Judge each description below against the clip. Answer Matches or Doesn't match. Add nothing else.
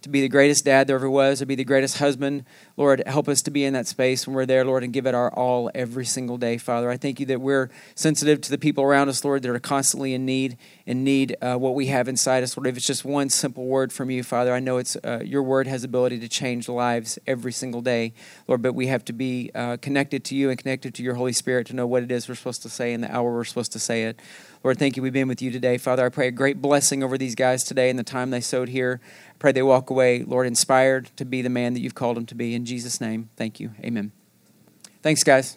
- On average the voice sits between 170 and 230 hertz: Doesn't match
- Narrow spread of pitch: Matches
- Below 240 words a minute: Doesn't match